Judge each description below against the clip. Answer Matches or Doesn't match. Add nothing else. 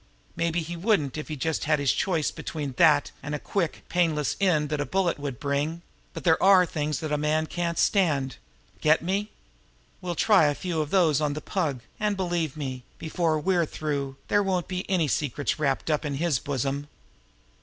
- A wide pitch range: Doesn't match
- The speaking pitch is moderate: Matches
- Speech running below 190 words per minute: Doesn't match